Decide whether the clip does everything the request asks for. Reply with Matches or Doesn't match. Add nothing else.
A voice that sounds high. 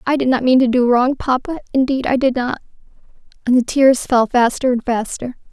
Matches